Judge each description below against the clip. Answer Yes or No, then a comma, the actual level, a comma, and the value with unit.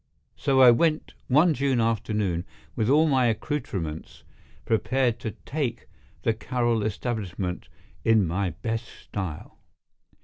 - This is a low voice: Yes, low, 115 Hz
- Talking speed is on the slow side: Yes, slow, 115 wpm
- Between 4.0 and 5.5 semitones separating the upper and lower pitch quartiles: Yes, average, 4.3 semitones